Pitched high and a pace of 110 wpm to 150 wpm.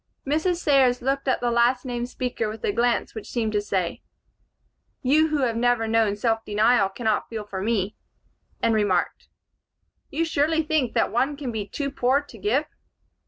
No: high, 240 Hz; average, 170 wpm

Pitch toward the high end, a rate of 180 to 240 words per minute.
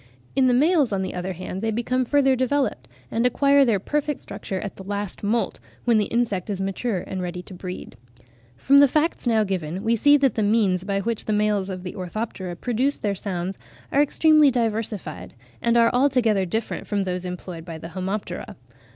Yes: high, 210 Hz; average, 195 wpm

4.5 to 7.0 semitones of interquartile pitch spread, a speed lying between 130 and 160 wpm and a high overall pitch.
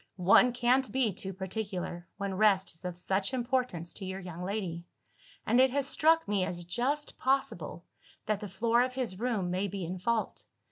No: average, 5.2 semitones; average, 185 wpm; high, 200 Hz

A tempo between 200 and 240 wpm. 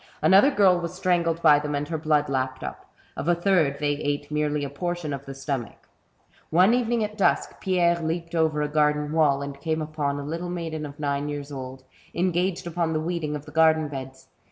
Yes: fast, 205 wpm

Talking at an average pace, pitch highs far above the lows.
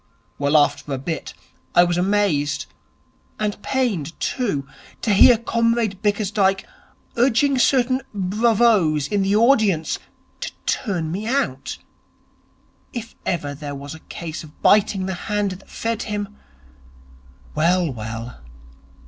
No: slow, 125 wpm; wide, 6.1 semitones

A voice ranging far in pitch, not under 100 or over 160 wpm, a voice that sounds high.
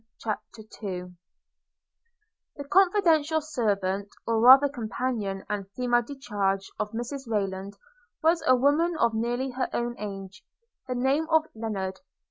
Yes: wide, 5.7 semitones; slow, 135 wpm; high, 235 Hz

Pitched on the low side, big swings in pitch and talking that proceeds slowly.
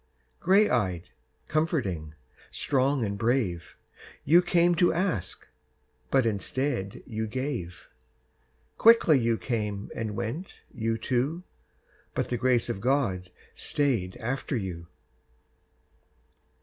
Yes: low, 120 Hz; wide, 6.0 semitones; slow, 100 wpm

